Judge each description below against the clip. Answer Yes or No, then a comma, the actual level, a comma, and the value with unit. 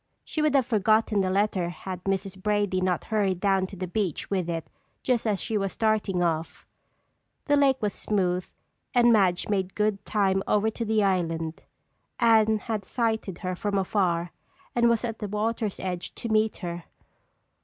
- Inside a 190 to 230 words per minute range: No, average, 175 wpm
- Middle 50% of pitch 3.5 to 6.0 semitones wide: No, average, 3.0 semitones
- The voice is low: No, high, 200 Hz